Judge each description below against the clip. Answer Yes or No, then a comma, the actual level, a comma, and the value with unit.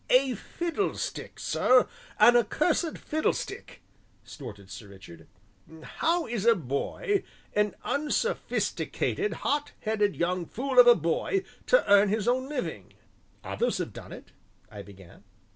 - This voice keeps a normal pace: No, slow, 125 wpm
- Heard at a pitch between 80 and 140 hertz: No, high, 230 Hz